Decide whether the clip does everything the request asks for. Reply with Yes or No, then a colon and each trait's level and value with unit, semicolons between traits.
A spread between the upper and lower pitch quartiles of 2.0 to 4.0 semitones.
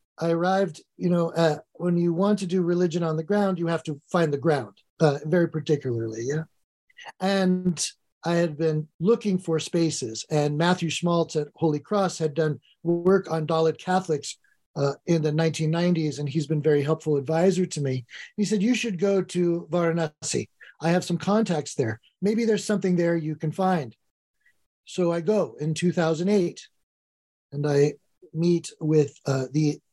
Yes: average, 3.0 semitones